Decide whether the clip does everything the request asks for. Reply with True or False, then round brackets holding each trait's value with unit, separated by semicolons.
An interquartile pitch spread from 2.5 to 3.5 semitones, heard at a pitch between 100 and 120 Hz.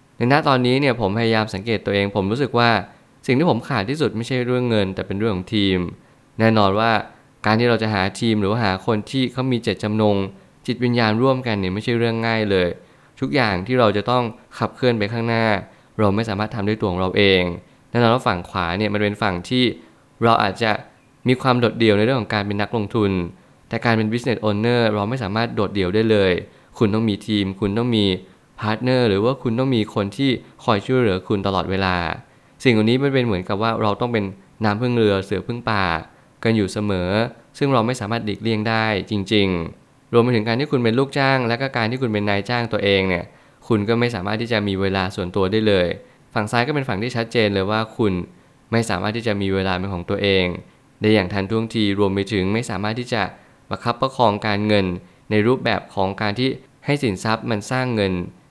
True (3.1 semitones; 110 Hz)